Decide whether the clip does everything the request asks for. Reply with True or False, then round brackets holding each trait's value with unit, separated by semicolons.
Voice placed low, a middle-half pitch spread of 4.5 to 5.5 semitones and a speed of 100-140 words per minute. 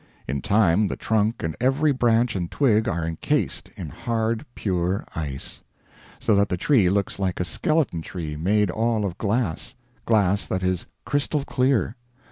False (105 Hz; 4.8 semitones; 160 wpm)